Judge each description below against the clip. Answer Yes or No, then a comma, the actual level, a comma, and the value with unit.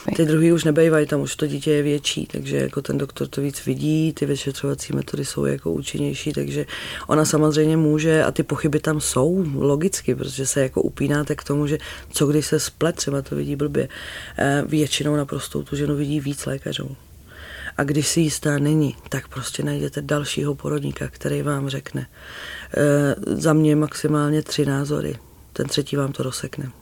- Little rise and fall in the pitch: Yes, narrow, 2.2 semitones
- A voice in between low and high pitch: Yes, medium, 145 Hz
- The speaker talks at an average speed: No, fast, 175 wpm